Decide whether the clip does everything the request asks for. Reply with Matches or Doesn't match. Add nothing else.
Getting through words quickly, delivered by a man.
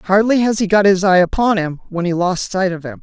Doesn't match